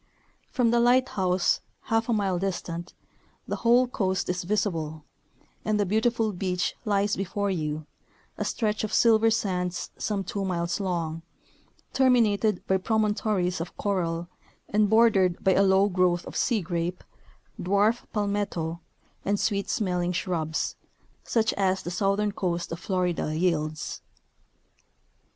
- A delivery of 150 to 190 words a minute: No, slow, 135 wpm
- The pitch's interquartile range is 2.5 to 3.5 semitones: Yes, average, 3.2 semitones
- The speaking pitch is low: No, high, 195 Hz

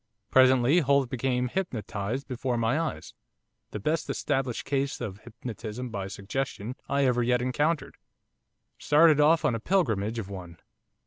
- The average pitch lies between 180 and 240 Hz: No, low, 125 Hz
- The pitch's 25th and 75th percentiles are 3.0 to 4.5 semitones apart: Yes, average, 3.8 semitones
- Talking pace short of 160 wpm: Yes, average, 140 wpm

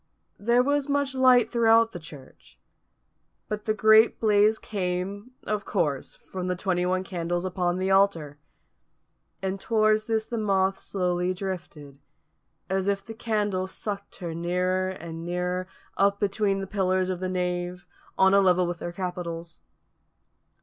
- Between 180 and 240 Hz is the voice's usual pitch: Yes, high, 190 Hz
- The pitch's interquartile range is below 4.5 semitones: Yes, average, 2.9 semitones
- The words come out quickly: No, average, 150 wpm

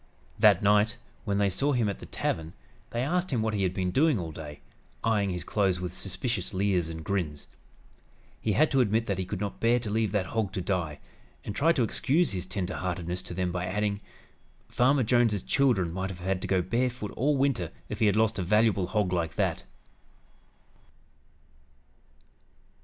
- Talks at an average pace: Yes, average, 190 wpm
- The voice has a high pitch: No, low, 100 Hz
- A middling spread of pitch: Yes, average, 4.1 semitones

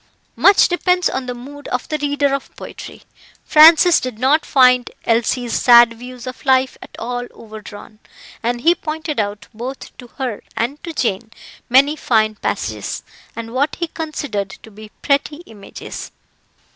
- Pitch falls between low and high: No, very high, 255 Hz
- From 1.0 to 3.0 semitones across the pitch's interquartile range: No, average, 4.2 semitones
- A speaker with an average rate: Yes, average, 155 wpm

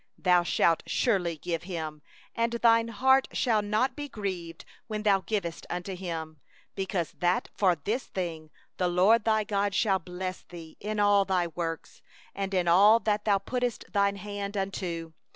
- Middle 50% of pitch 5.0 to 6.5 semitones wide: No, average, 3.4 semitones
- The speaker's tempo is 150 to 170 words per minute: Yes, average, 165 wpm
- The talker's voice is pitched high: Yes, high, 195 Hz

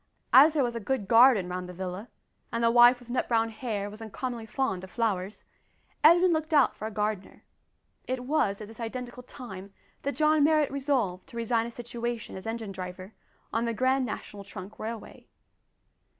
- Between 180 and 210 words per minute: Yes, average, 185 wpm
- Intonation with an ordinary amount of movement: Yes, average, 4.0 semitones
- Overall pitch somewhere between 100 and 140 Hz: No, high, 230 Hz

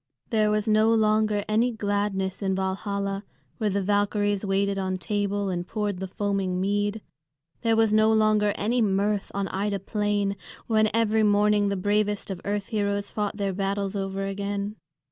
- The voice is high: Yes, high, 205 Hz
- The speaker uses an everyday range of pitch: No, narrow, 1.3 semitones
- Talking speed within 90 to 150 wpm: No, average, 165 wpm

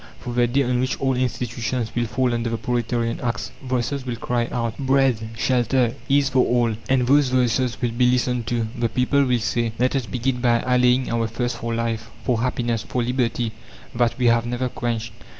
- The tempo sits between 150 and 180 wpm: No, average, 200 wpm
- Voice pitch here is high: No, low, 120 Hz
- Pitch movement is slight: Yes, narrow, 1.5 semitones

